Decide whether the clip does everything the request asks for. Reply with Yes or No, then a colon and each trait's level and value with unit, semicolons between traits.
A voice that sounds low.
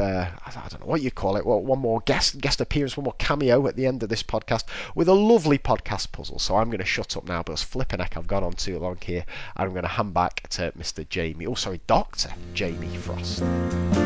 Yes: low, 100 Hz